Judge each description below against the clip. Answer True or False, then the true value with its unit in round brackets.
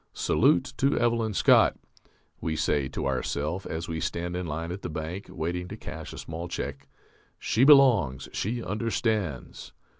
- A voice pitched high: False (85 Hz)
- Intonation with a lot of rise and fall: True (5.7 semitones)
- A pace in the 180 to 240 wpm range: False (155 wpm)